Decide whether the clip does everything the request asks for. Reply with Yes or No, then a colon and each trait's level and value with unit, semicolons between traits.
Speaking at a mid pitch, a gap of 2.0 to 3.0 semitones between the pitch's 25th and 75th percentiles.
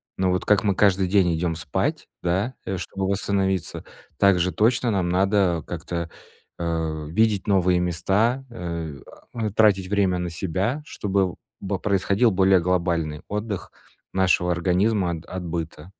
No: very low, 95 Hz; narrow, 2.6 semitones